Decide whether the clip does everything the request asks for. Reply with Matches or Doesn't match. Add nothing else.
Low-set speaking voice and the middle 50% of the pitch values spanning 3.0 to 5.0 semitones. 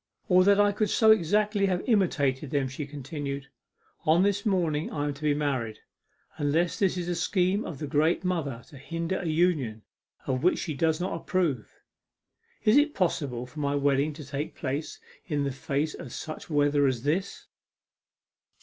Doesn't match